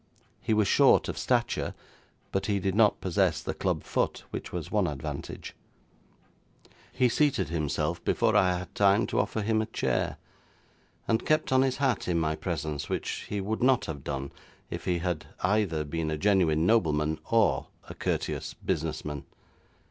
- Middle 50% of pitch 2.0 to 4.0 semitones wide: No, wide, 5.6 semitones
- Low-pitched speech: Yes, very low, 90 Hz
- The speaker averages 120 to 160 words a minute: No, average, 170 wpm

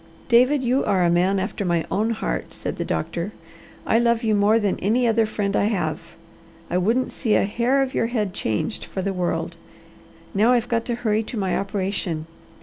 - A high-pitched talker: Yes, high, 210 Hz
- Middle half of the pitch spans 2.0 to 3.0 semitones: No, average, 3.8 semitones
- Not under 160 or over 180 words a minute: No, average, 200 wpm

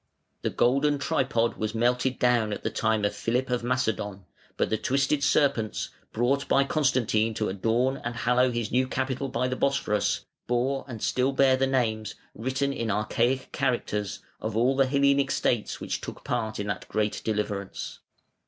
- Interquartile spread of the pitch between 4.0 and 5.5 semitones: No, average, 3.3 semitones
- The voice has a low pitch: Yes, low, 125 Hz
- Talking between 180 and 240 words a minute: No, average, 170 wpm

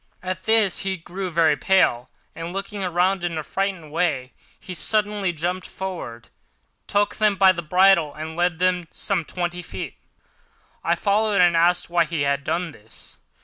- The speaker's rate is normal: Yes, average, 170 wpm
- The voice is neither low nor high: Yes, medium, 180 Hz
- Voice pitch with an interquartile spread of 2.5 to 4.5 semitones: Yes, average, 2.8 semitones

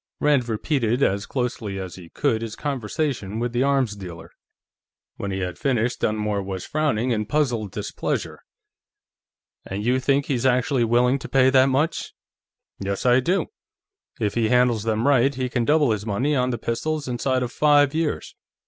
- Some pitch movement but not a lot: Yes, average, 4.3 semitones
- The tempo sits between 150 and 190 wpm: Yes, average, 170 wpm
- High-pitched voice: No, low, 125 Hz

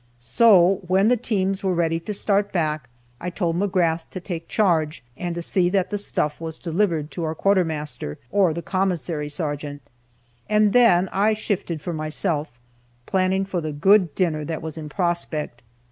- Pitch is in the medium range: Yes, medium, 175 Hz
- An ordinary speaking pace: Yes, average, 170 wpm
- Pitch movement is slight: No, average, 3.8 semitones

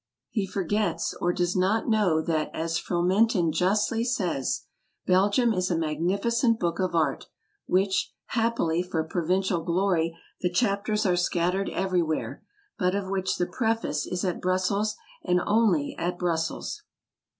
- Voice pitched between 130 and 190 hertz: Yes, medium, 185 Hz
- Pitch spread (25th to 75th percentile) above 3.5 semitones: No, average, 2.9 semitones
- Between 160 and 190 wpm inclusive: No, average, 140 wpm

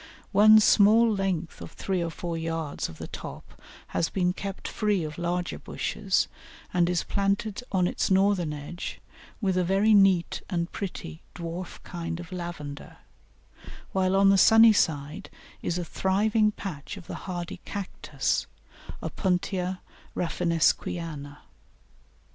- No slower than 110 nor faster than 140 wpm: Yes, slow, 135 wpm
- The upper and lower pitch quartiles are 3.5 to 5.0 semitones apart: No, average, 2.8 semitones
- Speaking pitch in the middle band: Yes, medium, 180 Hz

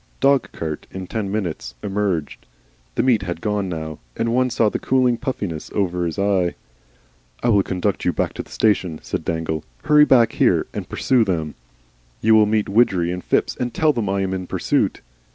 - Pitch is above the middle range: No, low, 100 Hz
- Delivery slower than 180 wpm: No, average, 190 wpm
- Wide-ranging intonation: No, average, 4.8 semitones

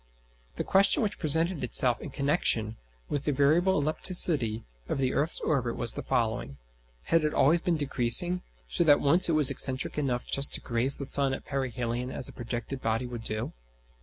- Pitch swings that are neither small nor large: Yes, average, 4.2 semitones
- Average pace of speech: Yes, average, 185 wpm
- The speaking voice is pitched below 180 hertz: Yes, low, 135 Hz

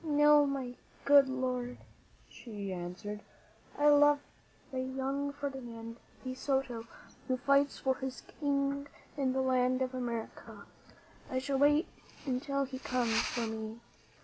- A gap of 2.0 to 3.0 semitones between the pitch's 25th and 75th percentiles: Yes, narrow, 2.4 semitones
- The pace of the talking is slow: Yes, slow, 130 wpm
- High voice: Yes, very high, 260 Hz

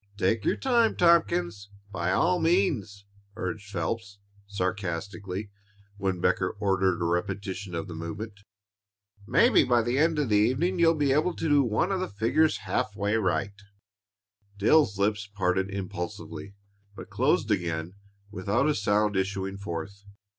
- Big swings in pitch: No, average, 4.9 semitones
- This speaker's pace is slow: No, average, 145 wpm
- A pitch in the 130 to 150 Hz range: No, low, 100 Hz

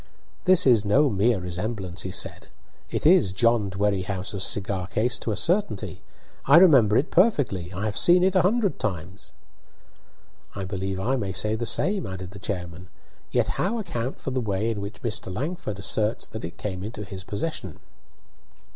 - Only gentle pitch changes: No, wide, 5.6 semitones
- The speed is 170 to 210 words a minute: Yes, average, 175 wpm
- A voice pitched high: No, low, 105 Hz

